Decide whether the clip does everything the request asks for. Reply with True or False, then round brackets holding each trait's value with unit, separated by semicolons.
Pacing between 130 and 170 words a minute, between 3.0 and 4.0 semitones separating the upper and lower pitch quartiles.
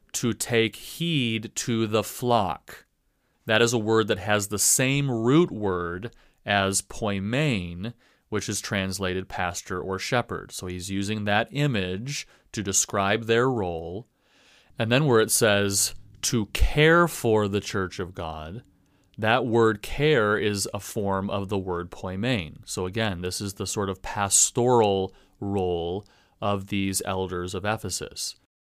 True (145 wpm; 3.4 semitones)